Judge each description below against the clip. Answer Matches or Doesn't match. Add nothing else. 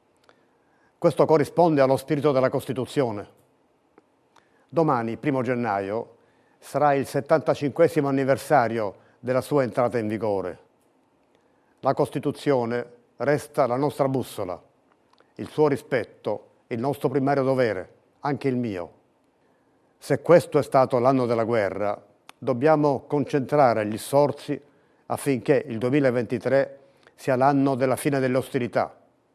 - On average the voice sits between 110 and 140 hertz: Matches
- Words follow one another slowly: Matches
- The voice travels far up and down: Doesn't match